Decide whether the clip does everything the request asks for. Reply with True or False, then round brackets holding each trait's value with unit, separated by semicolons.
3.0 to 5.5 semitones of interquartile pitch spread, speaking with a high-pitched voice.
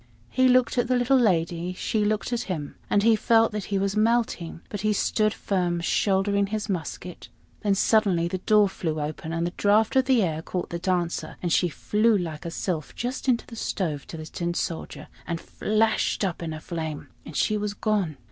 True (4.2 semitones; 195 Hz)